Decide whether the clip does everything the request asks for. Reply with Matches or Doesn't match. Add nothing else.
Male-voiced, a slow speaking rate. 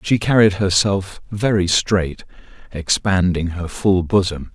Matches